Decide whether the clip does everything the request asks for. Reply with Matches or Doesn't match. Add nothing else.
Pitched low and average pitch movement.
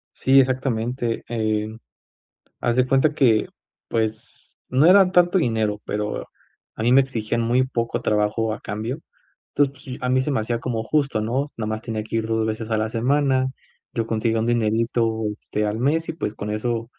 Matches